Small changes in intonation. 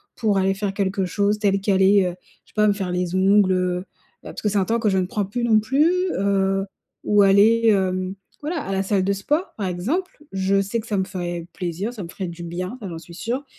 Yes: narrow, 2.2 semitones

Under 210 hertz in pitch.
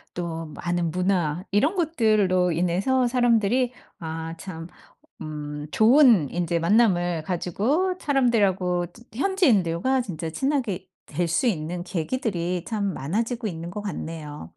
Yes: medium, 185 Hz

